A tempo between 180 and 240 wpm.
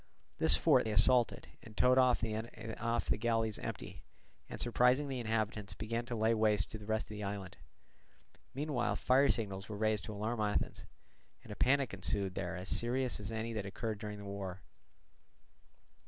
No: average, 170 wpm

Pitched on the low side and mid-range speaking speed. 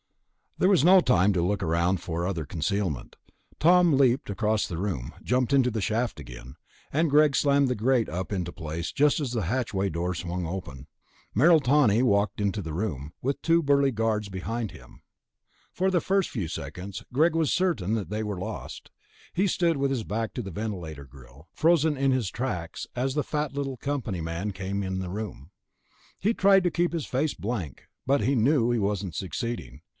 Yes: low, 110 Hz; average, 190 wpm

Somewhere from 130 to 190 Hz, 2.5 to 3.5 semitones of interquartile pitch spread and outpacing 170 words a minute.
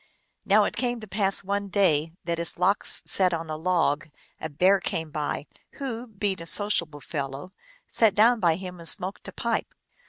No: medium, 185 Hz; average, 3.9 semitones; average, 185 wpm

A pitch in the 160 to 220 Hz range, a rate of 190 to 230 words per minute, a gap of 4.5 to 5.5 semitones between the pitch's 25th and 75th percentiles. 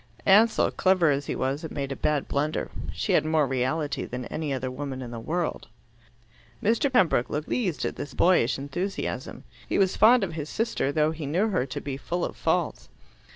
No: medium, 150 Hz; average, 200 wpm; average, 5.1 semitones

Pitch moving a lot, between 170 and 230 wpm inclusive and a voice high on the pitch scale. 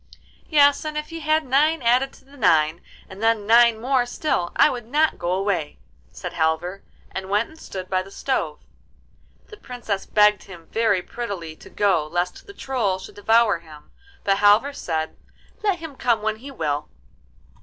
Yes: wide, 6.5 semitones; average, 175 wpm; high, 215 Hz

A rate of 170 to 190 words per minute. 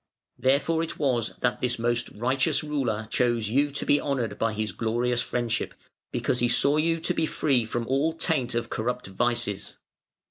Yes: average, 175 wpm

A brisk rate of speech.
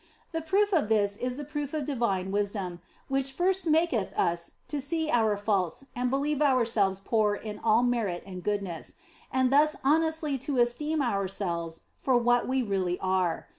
No: average, 170 wpm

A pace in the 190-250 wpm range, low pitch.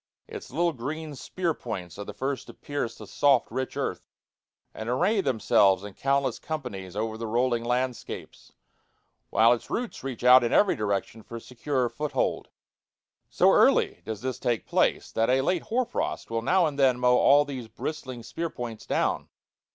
No: average, 175 wpm; low, 125 Hz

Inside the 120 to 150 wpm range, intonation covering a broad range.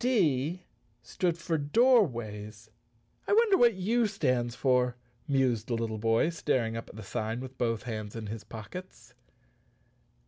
Yes: average, 145 wpm; wide, 8.0 semitones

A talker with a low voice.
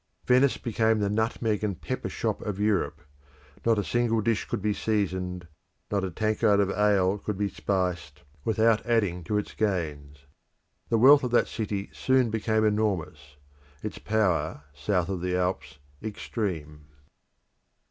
Yes: low, 105 Hz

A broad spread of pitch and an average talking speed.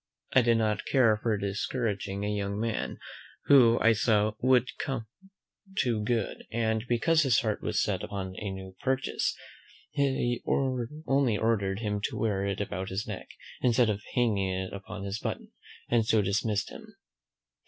No: average, 3.2 semitones; average, 160 wpm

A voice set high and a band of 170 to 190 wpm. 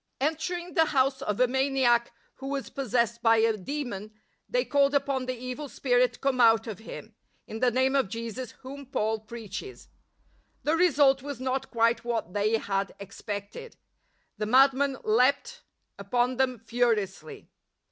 No: very high, 250 Hz; average, 160 wpm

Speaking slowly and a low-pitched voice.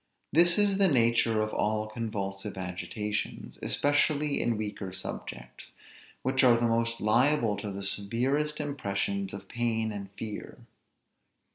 Yes: slow, 130 wpm; low, 110 Hz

